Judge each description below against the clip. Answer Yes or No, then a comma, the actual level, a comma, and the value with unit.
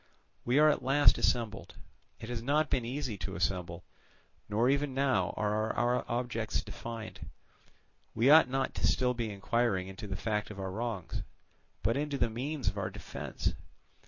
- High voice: No, low, 115 Hz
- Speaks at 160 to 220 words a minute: Yes, average, 165 wpm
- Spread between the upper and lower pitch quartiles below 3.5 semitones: No, average, 4.0 semitones